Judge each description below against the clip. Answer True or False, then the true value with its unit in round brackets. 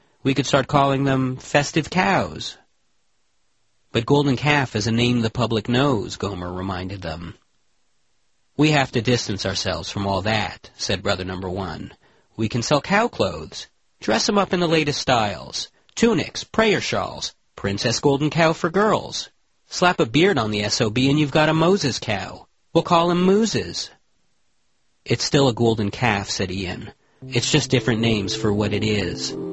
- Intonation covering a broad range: True (6.3 semitones)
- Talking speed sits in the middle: True (170 wpm)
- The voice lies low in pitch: True (120 Hz)